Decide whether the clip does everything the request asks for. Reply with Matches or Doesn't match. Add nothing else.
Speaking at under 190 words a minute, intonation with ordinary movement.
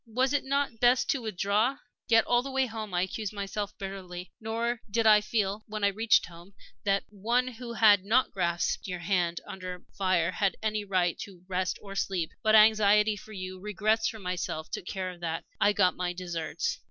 Doesn't match